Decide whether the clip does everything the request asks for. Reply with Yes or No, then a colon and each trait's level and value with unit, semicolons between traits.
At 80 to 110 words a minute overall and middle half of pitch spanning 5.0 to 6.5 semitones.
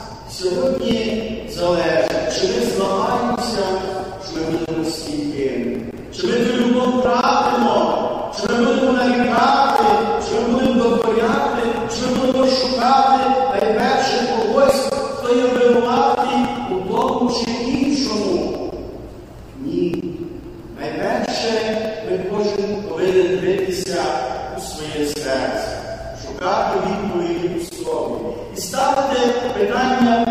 Yes: slow, 105 wpm; wide, 5.5 semitones